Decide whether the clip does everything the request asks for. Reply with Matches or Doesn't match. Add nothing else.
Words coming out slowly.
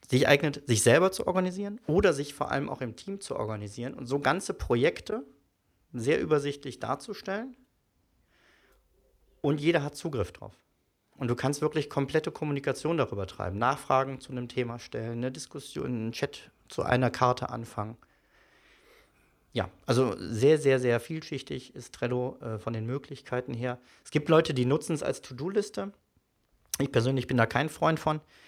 Doesn't match